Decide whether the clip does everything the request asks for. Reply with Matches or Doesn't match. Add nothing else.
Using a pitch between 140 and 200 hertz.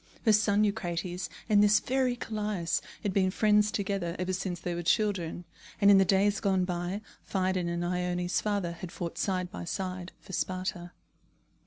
Matches